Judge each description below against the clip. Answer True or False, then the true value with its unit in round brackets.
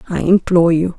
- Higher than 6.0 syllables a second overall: True (6.2 syllables/s)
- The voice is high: False (175 Hz)